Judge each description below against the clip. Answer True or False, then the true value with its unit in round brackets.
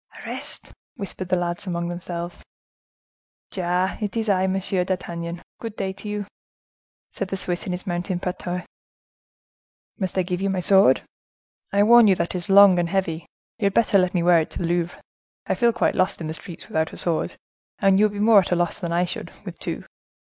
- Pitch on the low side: False (185 Hz)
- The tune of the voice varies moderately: False (2.2 semitones)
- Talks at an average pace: False (210 wpm)